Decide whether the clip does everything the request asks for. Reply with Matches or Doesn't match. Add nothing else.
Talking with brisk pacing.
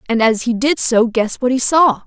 Matches